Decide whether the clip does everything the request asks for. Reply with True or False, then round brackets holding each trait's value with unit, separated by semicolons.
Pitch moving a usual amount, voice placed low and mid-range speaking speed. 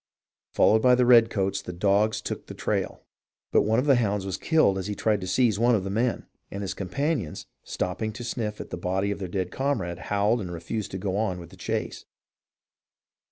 False (3.5 semitones; 105 Hz; 210 wpm)